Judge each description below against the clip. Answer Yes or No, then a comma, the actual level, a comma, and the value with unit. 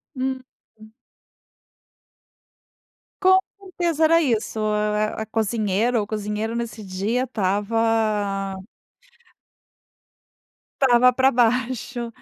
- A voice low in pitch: No, high, 225 Hz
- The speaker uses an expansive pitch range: No, average, 3.0 semitones